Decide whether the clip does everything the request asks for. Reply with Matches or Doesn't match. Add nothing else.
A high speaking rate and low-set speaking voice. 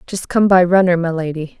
Doesn't match